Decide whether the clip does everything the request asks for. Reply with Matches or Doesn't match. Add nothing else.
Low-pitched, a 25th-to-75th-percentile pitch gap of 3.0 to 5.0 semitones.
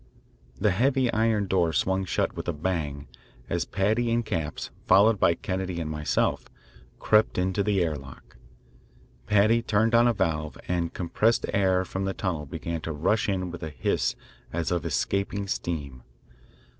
Matches